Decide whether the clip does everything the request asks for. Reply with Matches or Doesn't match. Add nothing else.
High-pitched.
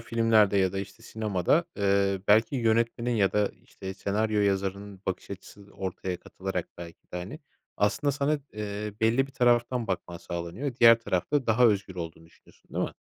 Doesn't match